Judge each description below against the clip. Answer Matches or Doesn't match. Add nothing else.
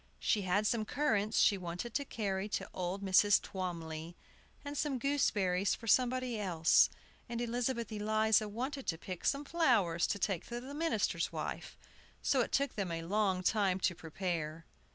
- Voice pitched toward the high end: Matches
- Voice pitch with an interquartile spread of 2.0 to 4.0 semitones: Doesn't match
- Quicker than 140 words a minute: Matches